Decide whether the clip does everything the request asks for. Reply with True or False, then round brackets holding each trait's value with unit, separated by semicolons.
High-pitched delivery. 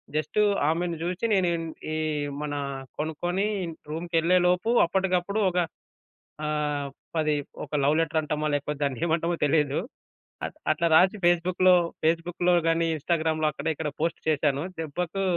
False (165 Hz)